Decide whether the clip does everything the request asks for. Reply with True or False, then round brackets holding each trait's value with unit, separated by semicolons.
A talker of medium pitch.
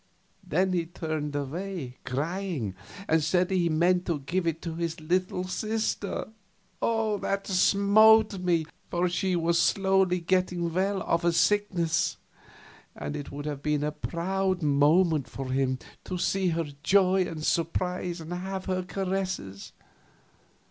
True (175 Hz)